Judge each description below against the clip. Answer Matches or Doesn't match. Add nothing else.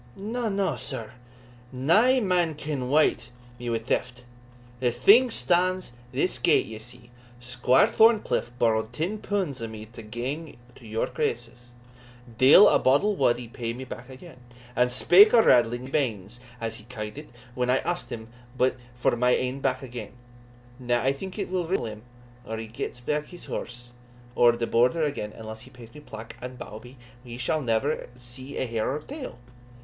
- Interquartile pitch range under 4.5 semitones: Doesn't match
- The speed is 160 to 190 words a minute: Matches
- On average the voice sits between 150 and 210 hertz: Doesn't match